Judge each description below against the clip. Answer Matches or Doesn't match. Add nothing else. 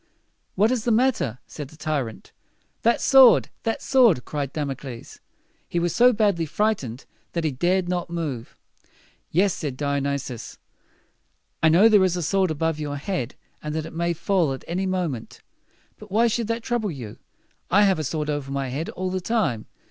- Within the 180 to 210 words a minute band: Matches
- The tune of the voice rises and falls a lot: Matches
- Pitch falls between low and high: Matches